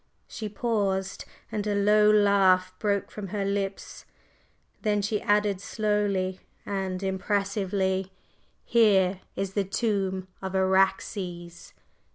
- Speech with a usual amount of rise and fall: No, narrow, 1.6 semitones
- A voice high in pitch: Yes, high, 195 Hz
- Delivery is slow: Yes, slow, 115 wpm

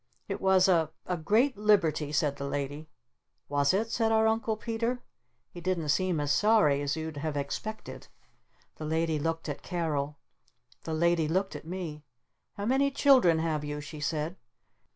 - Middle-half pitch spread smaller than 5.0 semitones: No, average, 5.3 semitones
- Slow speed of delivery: No, average, 165 wpm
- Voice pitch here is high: No, medium, 165 Hz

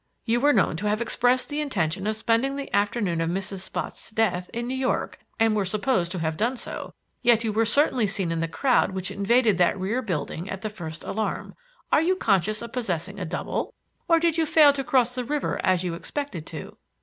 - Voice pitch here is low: No, high, 215 Hz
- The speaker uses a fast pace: Yes, fast, 220 wpm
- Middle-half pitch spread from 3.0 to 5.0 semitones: No, wide, 5.4 semitones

